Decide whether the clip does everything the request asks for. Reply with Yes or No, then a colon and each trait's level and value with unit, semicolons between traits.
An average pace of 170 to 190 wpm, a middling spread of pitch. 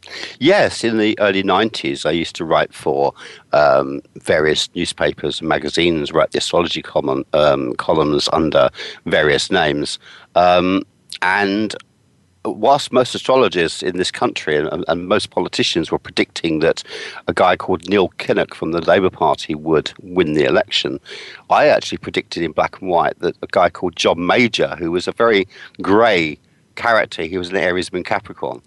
No: average, 160 wpm; average, 4.4 semitones